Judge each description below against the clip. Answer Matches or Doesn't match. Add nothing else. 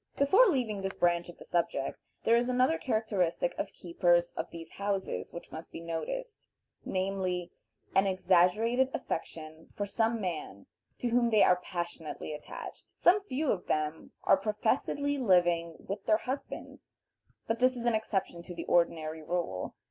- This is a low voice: Doesn't match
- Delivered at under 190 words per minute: Matches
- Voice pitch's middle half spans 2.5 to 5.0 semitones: Doesn't match